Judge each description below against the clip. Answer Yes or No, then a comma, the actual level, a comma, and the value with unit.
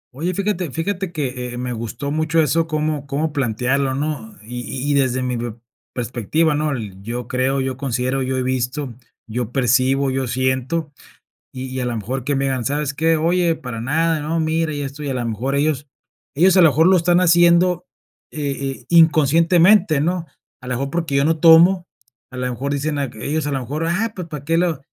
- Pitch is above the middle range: No, medium, 140 Hz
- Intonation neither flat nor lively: Yes, average, 4.1 semitones